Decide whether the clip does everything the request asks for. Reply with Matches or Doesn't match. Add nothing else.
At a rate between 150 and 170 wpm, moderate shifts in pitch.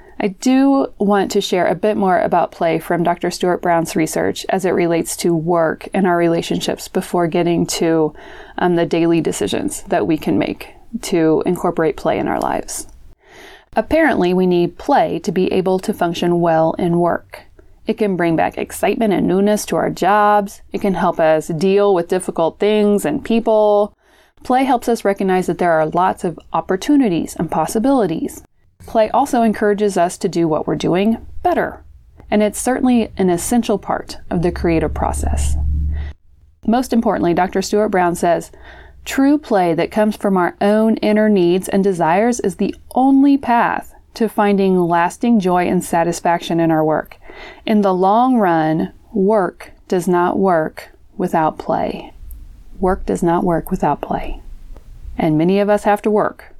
Matches